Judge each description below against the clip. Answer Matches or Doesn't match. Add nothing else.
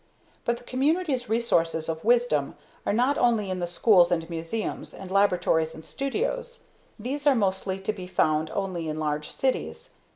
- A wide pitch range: Matches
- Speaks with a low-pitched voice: Doesn't match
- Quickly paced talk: Doesn't match